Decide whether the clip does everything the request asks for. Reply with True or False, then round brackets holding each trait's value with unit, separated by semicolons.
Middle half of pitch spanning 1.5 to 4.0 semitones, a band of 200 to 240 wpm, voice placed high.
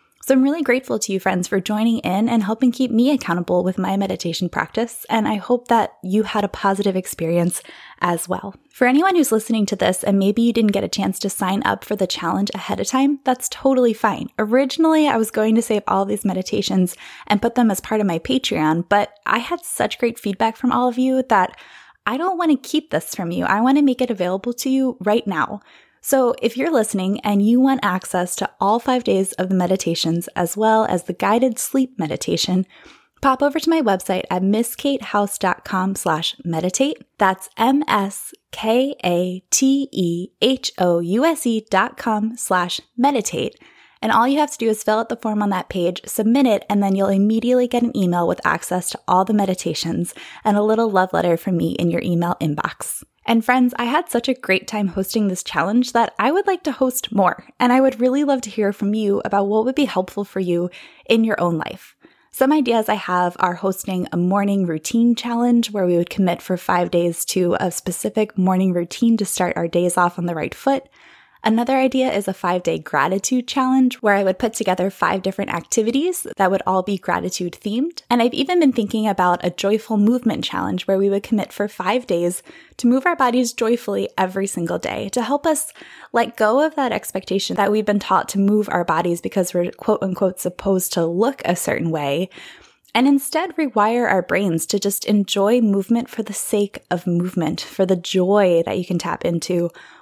False (4.8 semitones; 205 wpm; 210 Hz)